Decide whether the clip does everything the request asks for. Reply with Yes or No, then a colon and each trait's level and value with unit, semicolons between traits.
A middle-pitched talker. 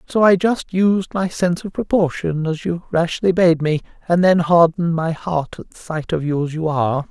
Yes: medium, 170 Hz